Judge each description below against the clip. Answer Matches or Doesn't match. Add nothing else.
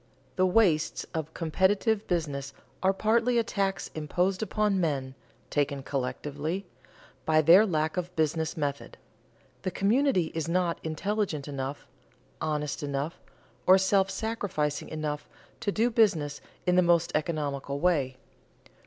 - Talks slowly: Matches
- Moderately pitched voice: Matches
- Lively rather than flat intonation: Doesn't match